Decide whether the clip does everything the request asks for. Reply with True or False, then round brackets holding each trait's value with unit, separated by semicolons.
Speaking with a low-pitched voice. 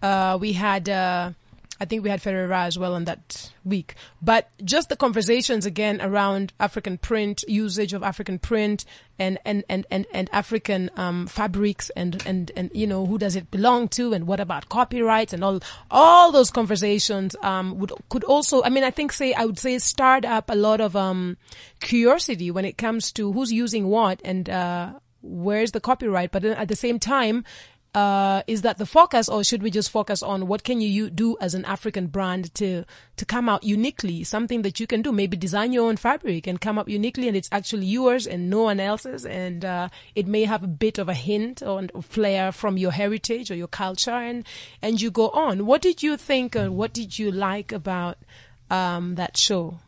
False (205 Hz)